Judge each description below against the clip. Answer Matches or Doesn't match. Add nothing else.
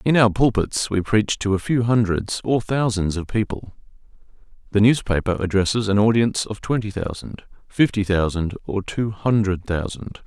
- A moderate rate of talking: Matches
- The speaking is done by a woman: Doesn't match